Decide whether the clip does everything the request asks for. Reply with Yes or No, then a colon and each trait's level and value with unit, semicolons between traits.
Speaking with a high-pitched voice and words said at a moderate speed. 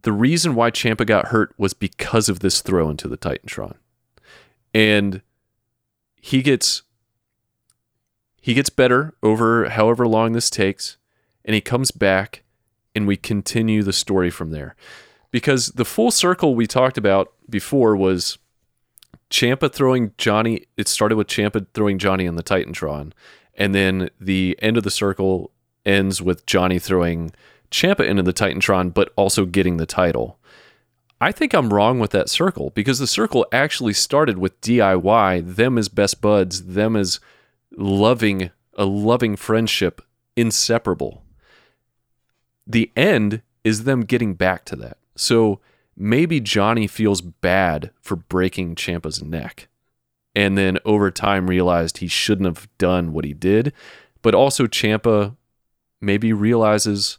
No: low, 105 Hz; average, 145 wpm